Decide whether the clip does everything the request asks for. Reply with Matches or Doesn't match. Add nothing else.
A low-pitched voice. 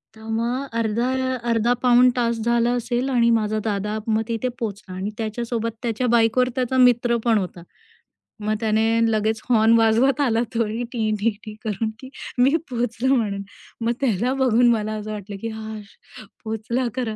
Doesn't match